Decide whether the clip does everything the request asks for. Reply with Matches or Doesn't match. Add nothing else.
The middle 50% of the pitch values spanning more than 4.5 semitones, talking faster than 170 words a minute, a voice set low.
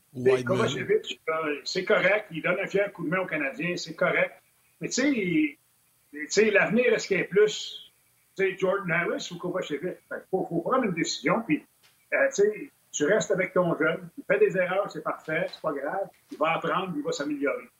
Doesn't match